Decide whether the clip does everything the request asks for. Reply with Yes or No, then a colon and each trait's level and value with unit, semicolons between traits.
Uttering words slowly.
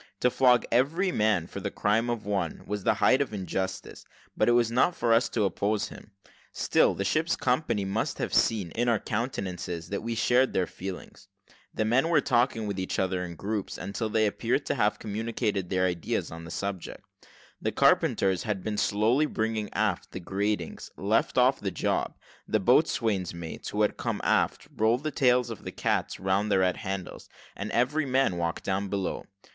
No: average, 195 wpm